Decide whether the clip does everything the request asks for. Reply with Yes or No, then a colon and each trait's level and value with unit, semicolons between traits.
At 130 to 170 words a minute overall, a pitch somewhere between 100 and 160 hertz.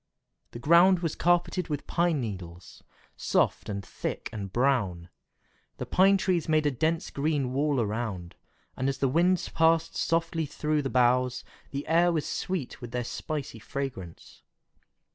Yes: average, 150 wpm; medium, 140 Hz